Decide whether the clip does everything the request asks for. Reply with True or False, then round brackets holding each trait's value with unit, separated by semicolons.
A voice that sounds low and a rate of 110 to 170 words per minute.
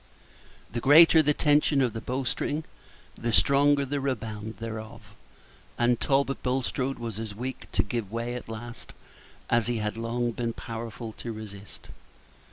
True (120 Hz; 150 wpm)